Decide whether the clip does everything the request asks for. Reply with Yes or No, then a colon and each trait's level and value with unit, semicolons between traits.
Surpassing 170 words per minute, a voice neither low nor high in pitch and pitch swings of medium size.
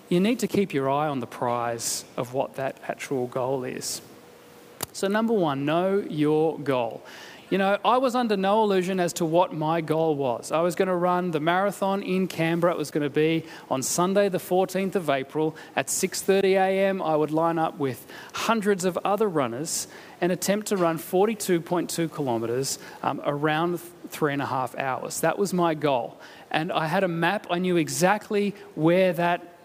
Yes: average, 185 wpm; medium, 175 Hz; average, 3.9 semitones